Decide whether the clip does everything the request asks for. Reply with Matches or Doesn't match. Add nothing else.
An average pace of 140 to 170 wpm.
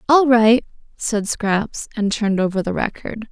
Matches